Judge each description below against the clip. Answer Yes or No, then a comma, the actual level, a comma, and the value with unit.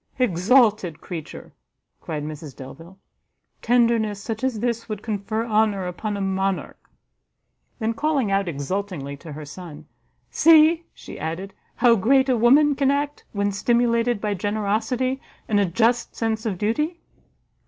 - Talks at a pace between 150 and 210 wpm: No, average, 140 wpm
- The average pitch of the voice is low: No, high, 215 Hz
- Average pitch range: Yes, average, 4.3 semitones